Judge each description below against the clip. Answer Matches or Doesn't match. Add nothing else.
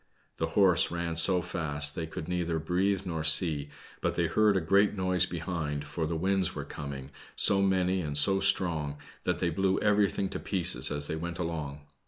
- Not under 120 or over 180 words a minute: Doesn't match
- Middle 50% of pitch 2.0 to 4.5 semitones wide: Matches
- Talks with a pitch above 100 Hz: Doesn't match